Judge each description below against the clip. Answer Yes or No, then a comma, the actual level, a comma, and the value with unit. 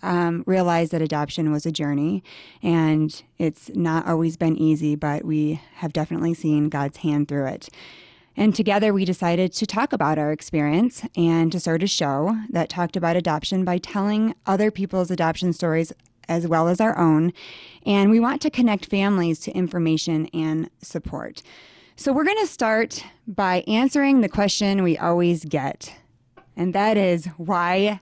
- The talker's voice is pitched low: No, medium, 170 Hz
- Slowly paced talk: No, average, 165 wpm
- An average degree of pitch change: Yes, average, 4.0 semitones